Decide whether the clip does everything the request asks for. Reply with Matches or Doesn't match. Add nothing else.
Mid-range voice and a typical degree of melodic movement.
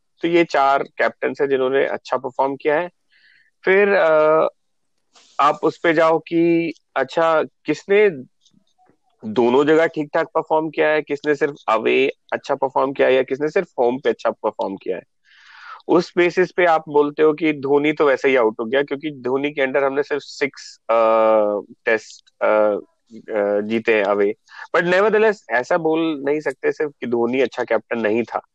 Matches